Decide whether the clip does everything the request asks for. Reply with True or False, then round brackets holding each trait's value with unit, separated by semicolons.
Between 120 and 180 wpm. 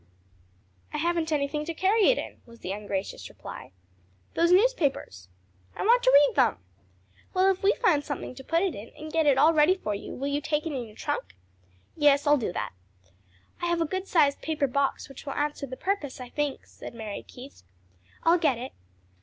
False (205 wpm)